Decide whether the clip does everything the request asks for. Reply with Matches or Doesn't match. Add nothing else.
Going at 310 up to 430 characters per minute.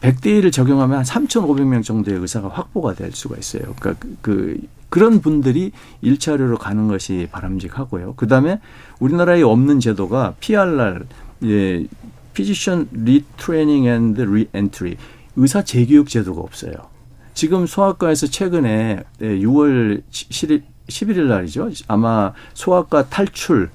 Matches